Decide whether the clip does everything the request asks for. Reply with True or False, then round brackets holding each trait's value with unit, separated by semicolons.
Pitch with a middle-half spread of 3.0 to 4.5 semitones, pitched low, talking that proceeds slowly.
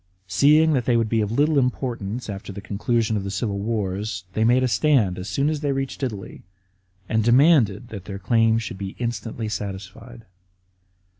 False (4.1 semitones; 115 Hz; 180 wpm)